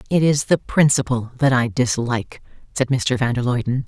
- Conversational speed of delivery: Yes, average, 185 wpm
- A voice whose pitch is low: Yes, low, 125 Hz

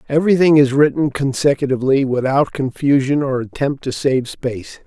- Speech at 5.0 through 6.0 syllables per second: Yes, 5.4 syllables/s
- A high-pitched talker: No, low, 135 Hz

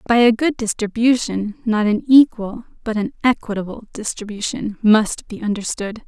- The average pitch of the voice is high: Yes, high, 220 Hz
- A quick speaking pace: No, average, 140 wpm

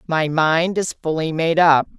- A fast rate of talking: No, average, 180 wpm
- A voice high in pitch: No, medium, 160 Hz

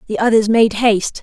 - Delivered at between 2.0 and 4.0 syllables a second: No, 5.7 syllables/s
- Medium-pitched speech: No, high, 220 Hz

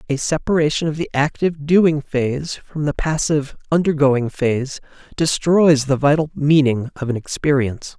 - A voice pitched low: No, medium, 145 Hz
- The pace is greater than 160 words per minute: No, average, 145 wpm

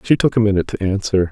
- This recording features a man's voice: Yes, male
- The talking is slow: No, fast, 275 wpm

